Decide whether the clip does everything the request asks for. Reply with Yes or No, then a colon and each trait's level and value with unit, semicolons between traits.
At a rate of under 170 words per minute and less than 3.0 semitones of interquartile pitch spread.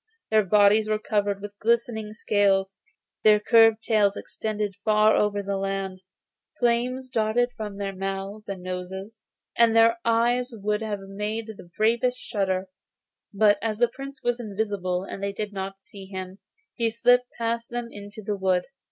Yes: average, 160 wpm; narrow, 2.6 semitones